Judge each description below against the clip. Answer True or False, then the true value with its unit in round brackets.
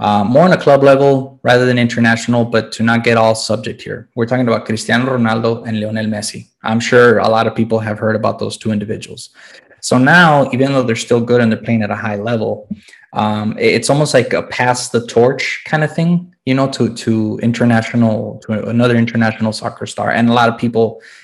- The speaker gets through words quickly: True (215 wpm)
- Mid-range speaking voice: False (115 Hz)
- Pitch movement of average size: False (2.1 semitones)